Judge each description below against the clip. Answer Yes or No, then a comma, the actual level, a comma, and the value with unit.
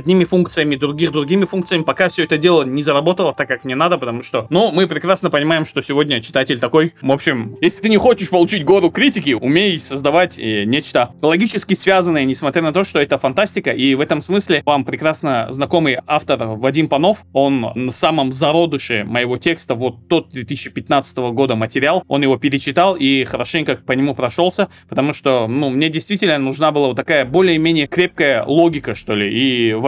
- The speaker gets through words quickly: Yes, fast, 180 wpm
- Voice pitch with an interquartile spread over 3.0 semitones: Yes, average, 4.6 semitones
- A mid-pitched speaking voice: Yes, medium, 150 Hz